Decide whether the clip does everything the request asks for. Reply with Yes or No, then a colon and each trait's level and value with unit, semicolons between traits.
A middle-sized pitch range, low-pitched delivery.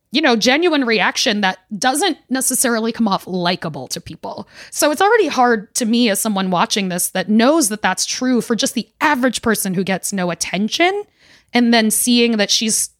No: average, 4.9 semitones; high, 230 Hz